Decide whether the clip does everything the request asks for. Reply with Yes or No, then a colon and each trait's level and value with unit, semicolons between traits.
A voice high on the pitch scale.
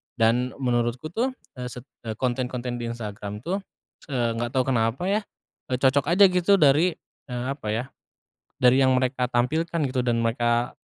No: low, 125 Hz